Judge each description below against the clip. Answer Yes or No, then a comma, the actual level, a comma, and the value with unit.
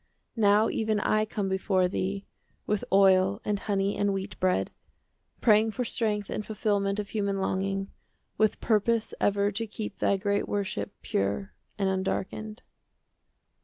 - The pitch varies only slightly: Yes, narrow, 1.6 semitones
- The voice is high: Yes, high, 200 Hz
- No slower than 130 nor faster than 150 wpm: Yes, average, 145 wpm